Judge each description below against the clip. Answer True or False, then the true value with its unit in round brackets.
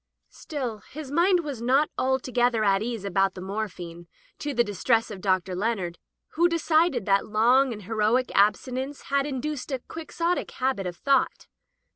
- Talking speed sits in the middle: True (155 wpm)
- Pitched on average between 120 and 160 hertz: False (240 Hz)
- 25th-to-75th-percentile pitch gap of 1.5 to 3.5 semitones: False (5.6 semitones)